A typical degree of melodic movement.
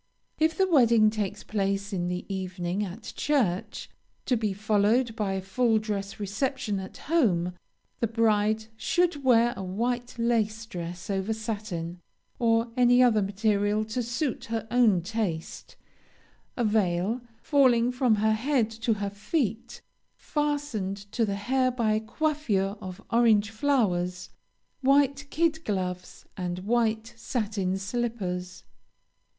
Yes: average, 3.6 semitones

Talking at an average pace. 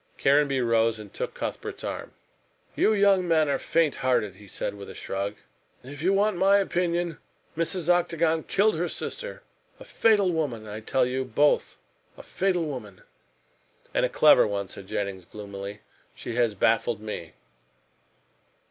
Yes: average, 155 wpm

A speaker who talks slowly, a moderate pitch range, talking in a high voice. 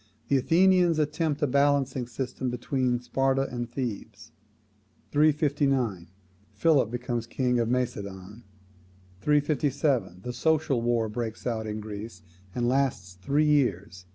No: slow, 120 wpm; average, 4.2 semitones; low, 125 Hz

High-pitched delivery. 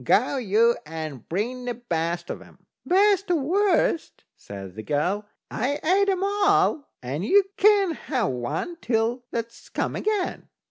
Yes: high, 245 Hz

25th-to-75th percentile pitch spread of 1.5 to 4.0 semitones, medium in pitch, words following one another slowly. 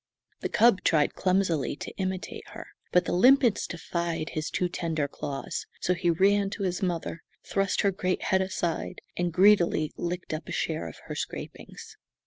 No: average, 2.8 semitones; medium, 180 Hz; average, 170 wpm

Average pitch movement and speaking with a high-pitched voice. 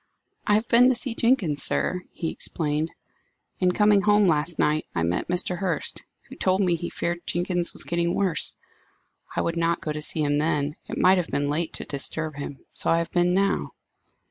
No: average, 3.7 semitones; medium, 170 Hz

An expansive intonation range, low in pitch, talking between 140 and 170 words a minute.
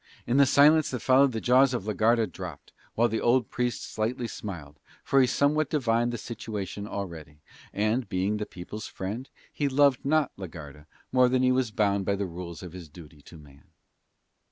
No: wide, 5.7 semitones; low, 110 Hz; average, 195 wpm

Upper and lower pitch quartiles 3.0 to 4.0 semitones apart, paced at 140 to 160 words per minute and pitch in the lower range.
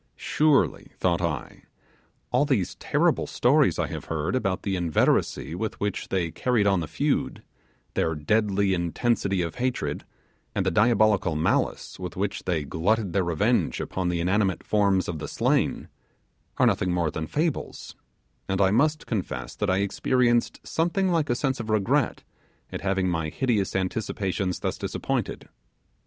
No: average, 4.8 semitones; average, 155 wpm; very low, 95 Hz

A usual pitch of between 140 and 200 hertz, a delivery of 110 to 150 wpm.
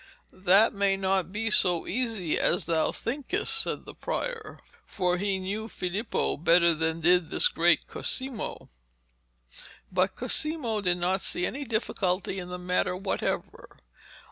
Yes: high, 190 Hz; average, 140 wpm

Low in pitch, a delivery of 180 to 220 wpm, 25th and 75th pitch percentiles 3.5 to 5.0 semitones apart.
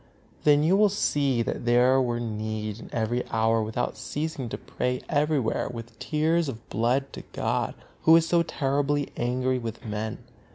No: low, 125 Hz; average, 160 wpm; average, 4.3 semitones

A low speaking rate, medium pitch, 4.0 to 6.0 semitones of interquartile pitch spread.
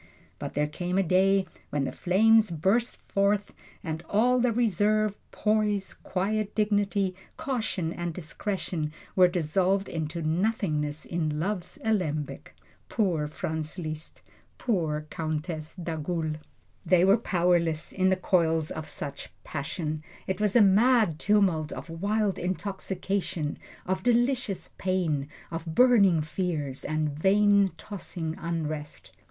Yes: slow, 125 wpm; medium, 180 Hz; average, 4.4 semitones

